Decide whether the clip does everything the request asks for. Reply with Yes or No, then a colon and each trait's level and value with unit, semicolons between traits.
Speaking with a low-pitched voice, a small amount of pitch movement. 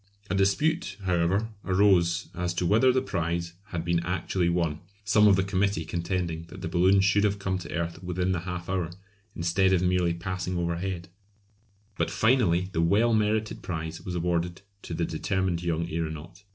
Yes: very low, 90 Hz; narrow, 2.3 semitones